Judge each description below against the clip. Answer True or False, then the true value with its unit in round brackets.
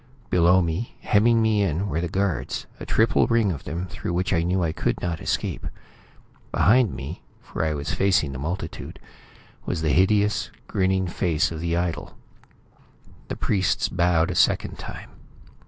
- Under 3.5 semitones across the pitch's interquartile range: True (3.1 semitones)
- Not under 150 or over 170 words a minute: True (165 wpm)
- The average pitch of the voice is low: True (90 Hz)